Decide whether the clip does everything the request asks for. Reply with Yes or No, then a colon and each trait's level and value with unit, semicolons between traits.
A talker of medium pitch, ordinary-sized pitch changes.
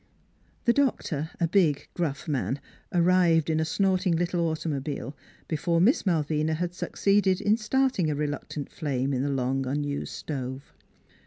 Yes: medium, 160 Hz; average, 4.2 semitones